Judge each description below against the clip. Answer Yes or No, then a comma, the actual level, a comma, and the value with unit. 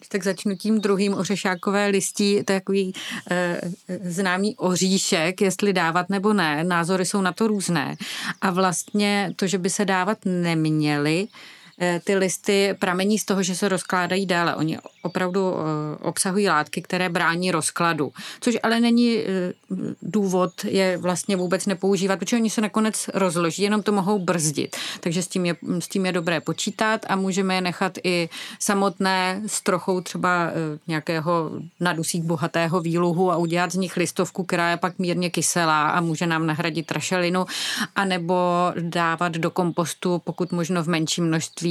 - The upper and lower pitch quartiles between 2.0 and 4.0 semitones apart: Yes, narrow, 2.5 semitones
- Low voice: No, medium, 185 Hz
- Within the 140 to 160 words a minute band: Yes, average, 155 wpm